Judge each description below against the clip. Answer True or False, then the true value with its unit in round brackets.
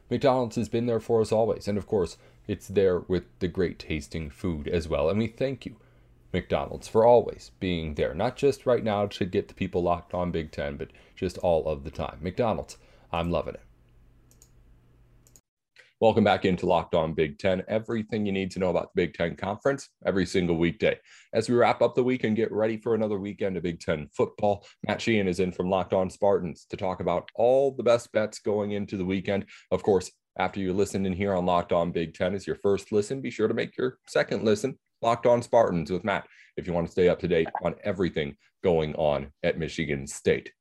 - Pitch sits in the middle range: False (100 Hz)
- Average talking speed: False (220 wpm)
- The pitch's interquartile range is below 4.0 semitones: False (4.8 semitones)